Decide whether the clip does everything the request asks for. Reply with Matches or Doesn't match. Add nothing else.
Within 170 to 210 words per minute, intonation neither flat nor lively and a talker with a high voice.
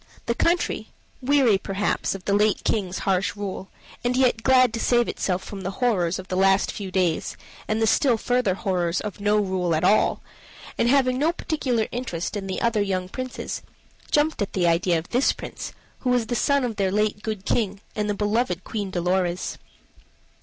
Matches